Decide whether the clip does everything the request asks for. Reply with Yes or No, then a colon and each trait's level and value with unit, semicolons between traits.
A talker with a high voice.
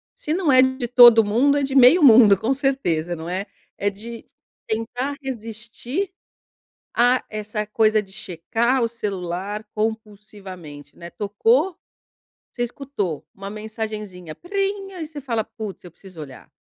Yes: high, 220 Hz